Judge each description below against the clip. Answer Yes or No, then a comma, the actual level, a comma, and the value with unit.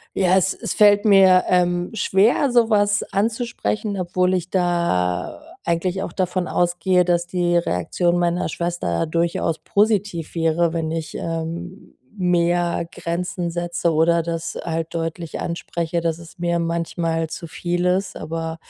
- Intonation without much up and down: Yes, narrow, 1.7 semitones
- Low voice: No, medium, 175 Hz